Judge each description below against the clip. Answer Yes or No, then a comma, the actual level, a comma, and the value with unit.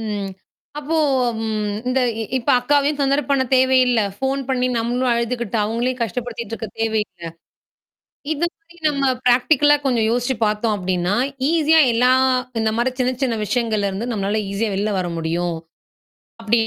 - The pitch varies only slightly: No, average, 3.6 semitones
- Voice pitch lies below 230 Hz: No, high, 235 Hz